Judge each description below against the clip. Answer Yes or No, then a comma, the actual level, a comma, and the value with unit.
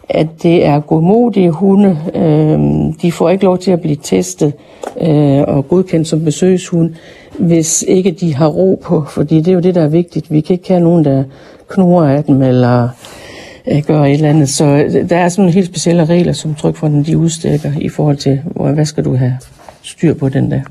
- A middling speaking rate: Yes, average, 200 wpm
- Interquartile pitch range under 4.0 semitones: Yes, average, 3.4 semitones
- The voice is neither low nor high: Yes, medium, 160 Hz